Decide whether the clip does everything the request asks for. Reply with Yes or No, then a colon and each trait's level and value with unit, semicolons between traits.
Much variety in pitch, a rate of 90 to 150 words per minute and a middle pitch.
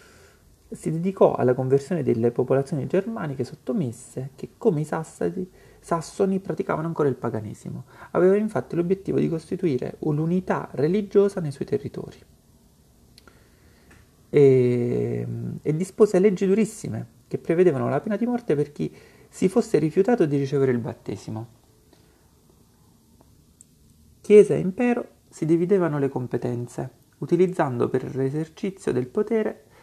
Yes: wide, 7.5 semitones; average, 120 wpm; medium, 155 Hz